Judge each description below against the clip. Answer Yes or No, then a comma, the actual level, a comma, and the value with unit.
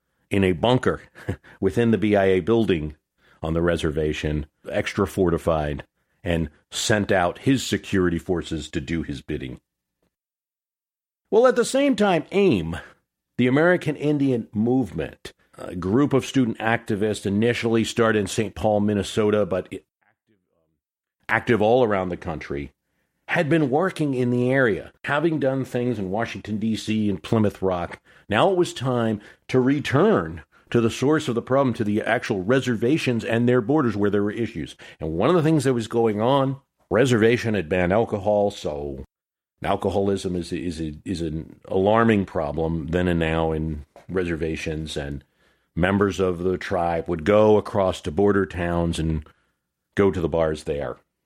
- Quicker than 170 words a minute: No, average, 155 wpm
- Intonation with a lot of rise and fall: Yes, wide, 6.1 semitones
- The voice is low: Yes, low, 105 Hz